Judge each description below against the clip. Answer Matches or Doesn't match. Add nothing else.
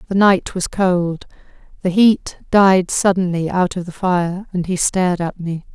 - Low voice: Doesn't match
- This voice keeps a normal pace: Matches